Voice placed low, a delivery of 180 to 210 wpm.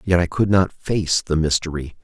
Yes: very low, 85 Hz; fast, 205 wpm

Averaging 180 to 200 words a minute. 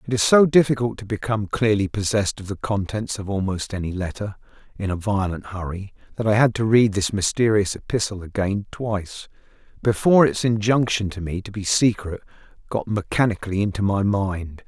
No: average, 170 wpm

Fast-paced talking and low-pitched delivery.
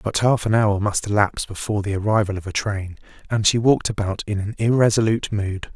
Yes: fast, 210 wpm; low, 105 Hz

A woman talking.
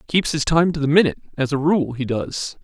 No: male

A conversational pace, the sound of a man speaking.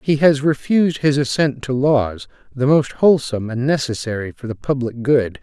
Yes: average, 175 wpm; male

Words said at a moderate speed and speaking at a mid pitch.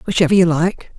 Yes: average, 185 wpm; medium, 175 Hz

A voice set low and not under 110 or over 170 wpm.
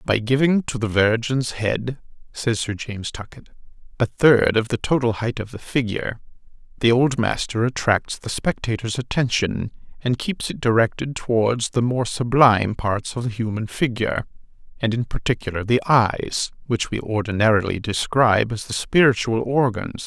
Yes: low, 115 Hz; average, 155 wpm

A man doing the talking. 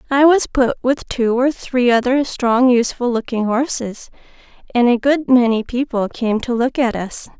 No: female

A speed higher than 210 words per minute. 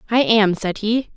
No: fast, 205 wpm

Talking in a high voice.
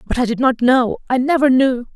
Yes: very high, 255 Hz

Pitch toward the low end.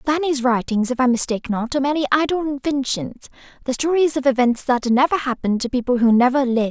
No: very high, 260 Hz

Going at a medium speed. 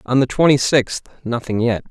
Yes: average, 190 wpm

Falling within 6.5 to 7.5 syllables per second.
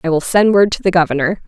Yes: 6.6 syllables/s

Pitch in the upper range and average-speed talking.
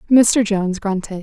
Yes: high, 205 Hz; average, 145 wpm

